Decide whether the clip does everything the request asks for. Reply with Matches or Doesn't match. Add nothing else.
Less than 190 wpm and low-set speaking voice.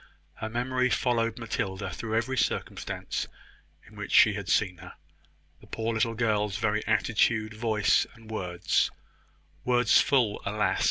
Matches